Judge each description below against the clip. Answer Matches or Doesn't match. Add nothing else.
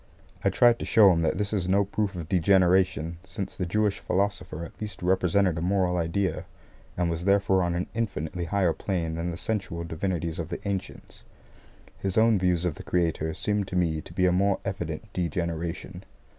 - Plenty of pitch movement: Doesn't match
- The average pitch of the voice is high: Doesn't match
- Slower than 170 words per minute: Doesn't match